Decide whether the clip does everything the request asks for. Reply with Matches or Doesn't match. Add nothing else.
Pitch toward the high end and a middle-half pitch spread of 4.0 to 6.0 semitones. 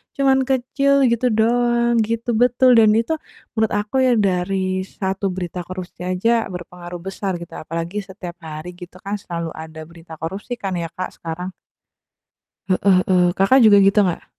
Matches